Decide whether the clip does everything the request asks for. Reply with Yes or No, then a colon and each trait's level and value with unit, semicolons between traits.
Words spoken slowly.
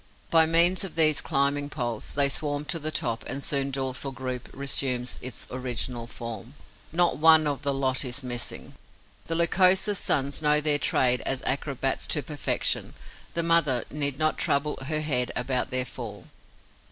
No: average, 165 wpm